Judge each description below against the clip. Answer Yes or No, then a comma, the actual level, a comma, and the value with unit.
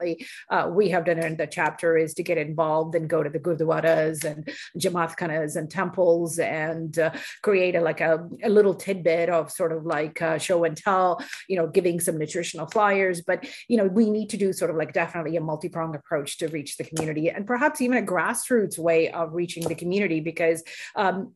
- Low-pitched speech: No, medium, 170 Hz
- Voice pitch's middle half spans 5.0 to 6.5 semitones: No, narrow, 2.5 semitones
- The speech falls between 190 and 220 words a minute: Yes, average, 200 wpm